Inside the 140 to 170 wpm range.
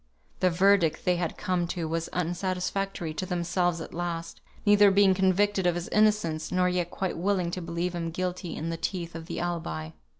No: average, 190 wpm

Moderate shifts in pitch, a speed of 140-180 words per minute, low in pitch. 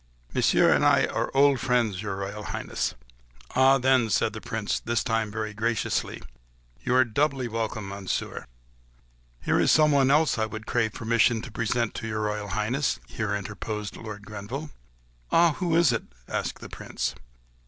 Yes: average, 3.6 semitones; average, 165 wpm; low, 115 Hz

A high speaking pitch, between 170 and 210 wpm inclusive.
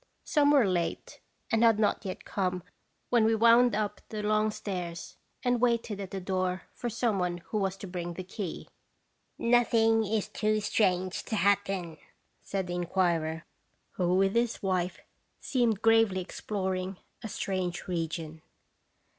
No: high, 195 Hz; average, 155 wpm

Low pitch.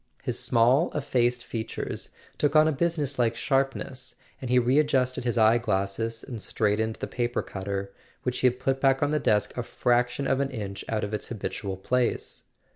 Yes: low, 125 Hz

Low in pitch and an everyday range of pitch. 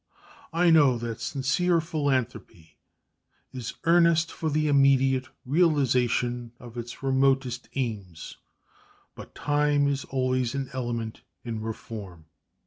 Yes: low, 130 Hz; average, 3.5 semitones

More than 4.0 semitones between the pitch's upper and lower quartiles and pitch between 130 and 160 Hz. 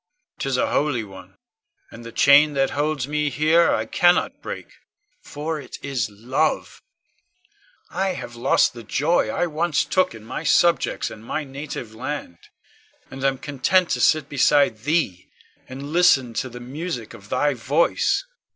Yes: average, 4.4 semitones; medium, 140 Hz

